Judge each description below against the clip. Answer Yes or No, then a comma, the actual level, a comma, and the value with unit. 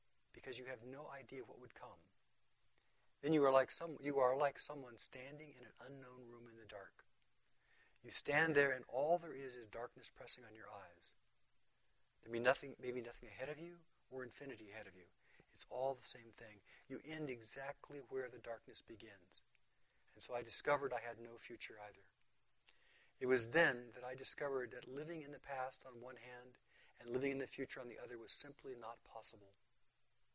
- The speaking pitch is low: Yes, low, 130 Hz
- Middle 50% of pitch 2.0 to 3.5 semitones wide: Yes, average, 2.8 semitones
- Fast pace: No, average, 195 wpm